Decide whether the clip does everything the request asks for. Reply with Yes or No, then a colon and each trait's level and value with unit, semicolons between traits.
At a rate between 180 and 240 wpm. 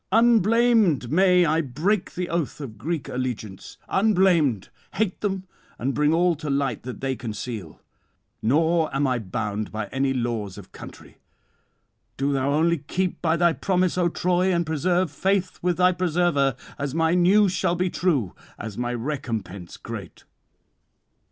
No: average, 155 wpm